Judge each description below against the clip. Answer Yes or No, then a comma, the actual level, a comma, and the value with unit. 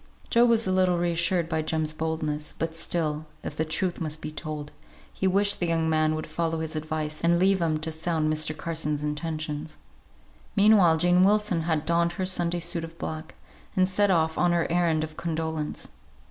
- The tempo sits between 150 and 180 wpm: No, average, 190 wpm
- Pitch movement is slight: Yes, narrow, 2.0 semitones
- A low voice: No, medium, 165 Hz